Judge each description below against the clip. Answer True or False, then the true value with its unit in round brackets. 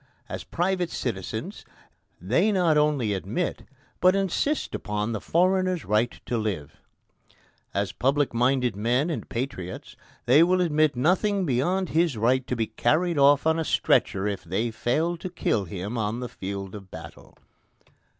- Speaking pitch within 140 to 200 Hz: False (130 Hz)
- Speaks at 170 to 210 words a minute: False (150 wpm)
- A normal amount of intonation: False (8.2 semitones)